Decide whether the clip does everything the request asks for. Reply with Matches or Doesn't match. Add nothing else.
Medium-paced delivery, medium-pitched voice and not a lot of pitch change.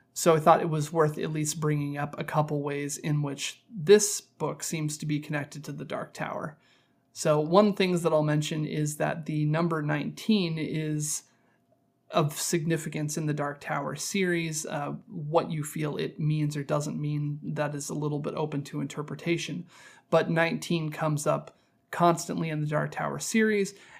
Matches